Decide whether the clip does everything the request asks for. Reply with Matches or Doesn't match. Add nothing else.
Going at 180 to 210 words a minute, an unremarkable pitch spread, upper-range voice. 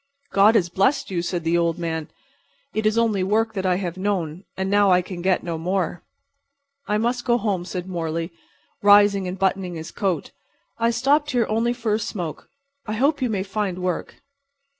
Matches